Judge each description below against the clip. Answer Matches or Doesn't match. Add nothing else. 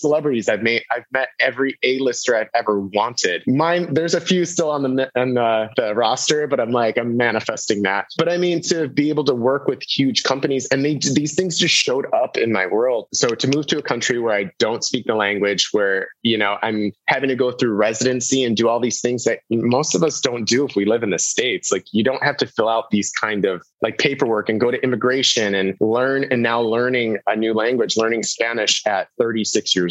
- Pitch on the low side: Matches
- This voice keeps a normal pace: Doesn't match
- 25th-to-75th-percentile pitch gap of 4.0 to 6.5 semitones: Matches